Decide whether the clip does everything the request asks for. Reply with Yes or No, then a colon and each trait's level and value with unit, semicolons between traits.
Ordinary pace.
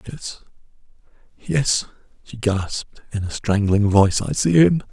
No: slow, 120 wpm